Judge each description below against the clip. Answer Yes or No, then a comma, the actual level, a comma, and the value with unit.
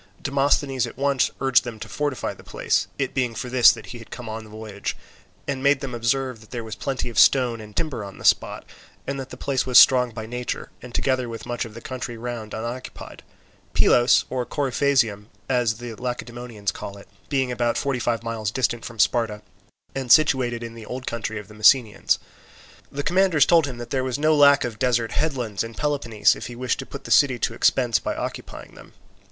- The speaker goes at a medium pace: No, fast, 210 wpm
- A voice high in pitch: No, low, 120 Hz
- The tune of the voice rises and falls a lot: No, average, 2.7 semitones